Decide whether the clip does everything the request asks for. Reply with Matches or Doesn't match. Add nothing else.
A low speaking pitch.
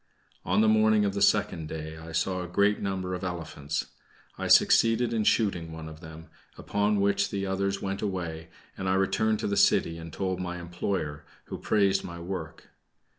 Matches